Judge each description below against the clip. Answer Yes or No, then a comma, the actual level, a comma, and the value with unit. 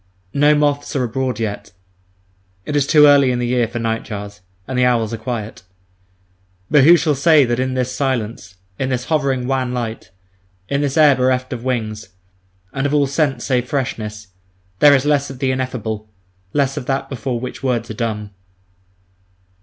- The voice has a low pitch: Yes, low, 130 Hz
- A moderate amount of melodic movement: Yes, average, 3.2 semitones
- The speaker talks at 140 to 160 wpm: No, average, 175 wpm